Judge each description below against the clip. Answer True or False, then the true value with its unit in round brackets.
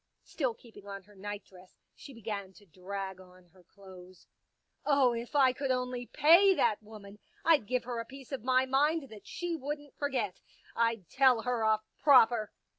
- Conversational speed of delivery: True (180 wpm)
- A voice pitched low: False (230 Hz)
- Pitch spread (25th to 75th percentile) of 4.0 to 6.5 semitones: True (5.0 semitones)